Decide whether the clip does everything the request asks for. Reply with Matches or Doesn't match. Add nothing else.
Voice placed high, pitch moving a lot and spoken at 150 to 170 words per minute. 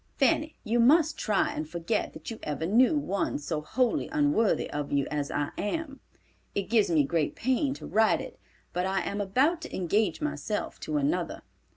Doesn't match